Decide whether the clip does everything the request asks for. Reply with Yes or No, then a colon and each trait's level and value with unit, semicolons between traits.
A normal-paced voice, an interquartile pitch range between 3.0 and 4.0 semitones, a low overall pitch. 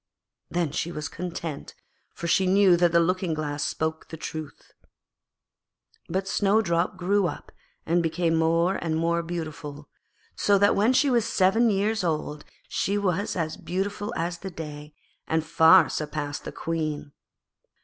No: average, 150 wpm; average, 3.3 semitones; medium, 170 Hz